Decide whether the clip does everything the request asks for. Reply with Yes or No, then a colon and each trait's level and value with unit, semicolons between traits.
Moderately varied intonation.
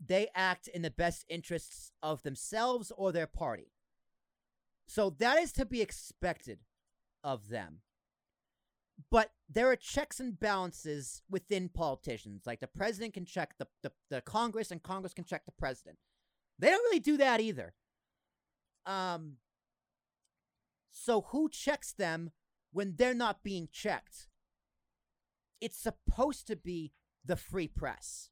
No: wide, 7.2 semitones